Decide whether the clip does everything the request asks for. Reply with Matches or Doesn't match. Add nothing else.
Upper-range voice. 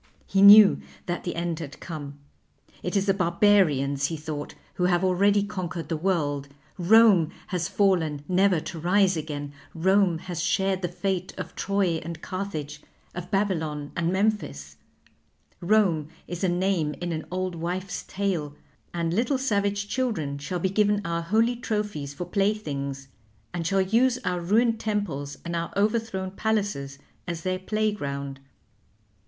Doesn't match